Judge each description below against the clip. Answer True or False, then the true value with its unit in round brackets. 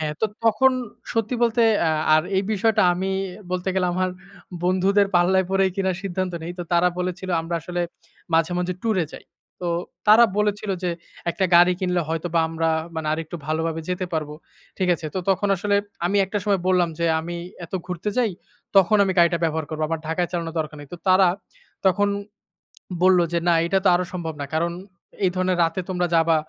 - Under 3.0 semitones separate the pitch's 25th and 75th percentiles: True (2.5 semitones)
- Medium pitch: True (180 Hz)